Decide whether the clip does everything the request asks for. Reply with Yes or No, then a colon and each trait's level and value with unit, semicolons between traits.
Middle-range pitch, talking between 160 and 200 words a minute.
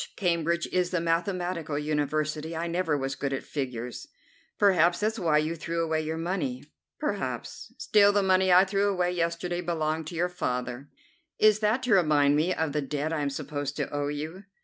Yes: medium, 165 Hz; average, 185 wpm